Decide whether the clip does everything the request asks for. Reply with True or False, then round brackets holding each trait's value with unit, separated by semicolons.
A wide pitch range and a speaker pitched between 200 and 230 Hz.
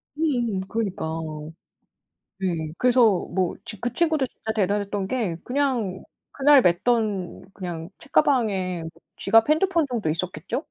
True (5.8 semitones; 215 Hz)